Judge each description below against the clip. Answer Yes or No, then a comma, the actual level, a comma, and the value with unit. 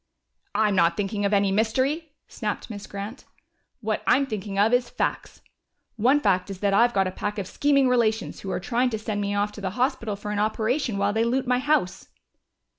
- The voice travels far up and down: No, average, 3.6 semitones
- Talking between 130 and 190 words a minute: No, fast, 205 wpm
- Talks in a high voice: Yes, high, 215 Hz